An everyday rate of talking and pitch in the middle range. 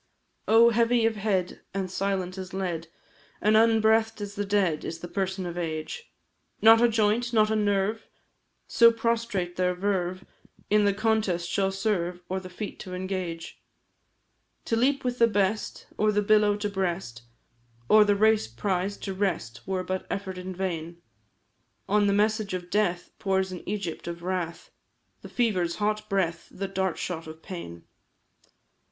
No: average, 160 wpm; high, 195 Hz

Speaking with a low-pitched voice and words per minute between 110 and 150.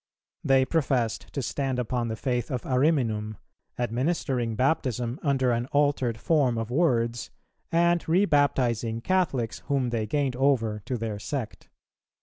Yes: low, 125 Hz; slow, 135 wpm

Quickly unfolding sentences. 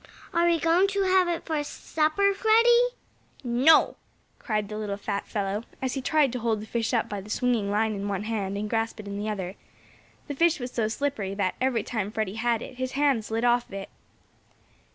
Yes: fast, 215 wpm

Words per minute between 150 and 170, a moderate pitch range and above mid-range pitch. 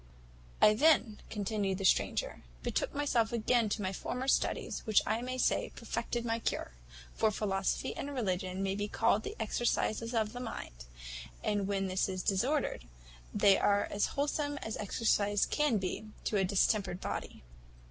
Yes: average, 160 wpm; average, 3.5 semitones; high, 215 Hz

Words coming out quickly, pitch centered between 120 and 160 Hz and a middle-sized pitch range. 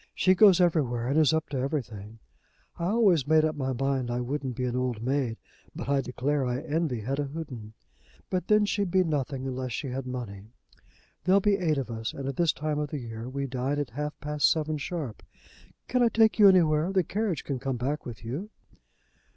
Yes: fast, 210 wpm; medium, 140 Hz; average, 4.5 semitones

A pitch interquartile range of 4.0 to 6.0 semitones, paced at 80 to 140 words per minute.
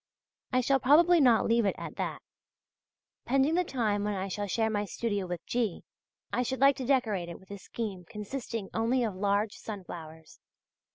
No: average, 4.3 semitones; average, 180 wpm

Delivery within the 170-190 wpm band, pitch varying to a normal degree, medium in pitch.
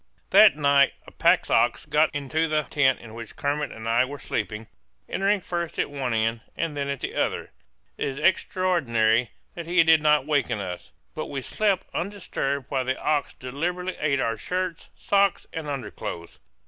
Yes: average, 175 wpm; average, 5.0 semitones; medium, 145 Hz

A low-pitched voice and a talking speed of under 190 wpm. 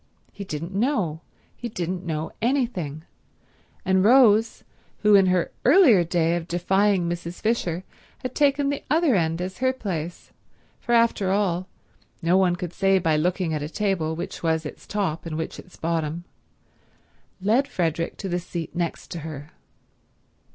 No: medium, 180 Hz; average, 155 wpm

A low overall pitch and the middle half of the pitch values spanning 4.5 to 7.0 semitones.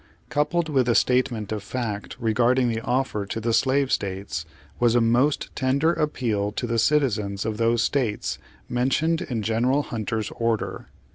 No: low, 120 Hz; average, 3.3 semitones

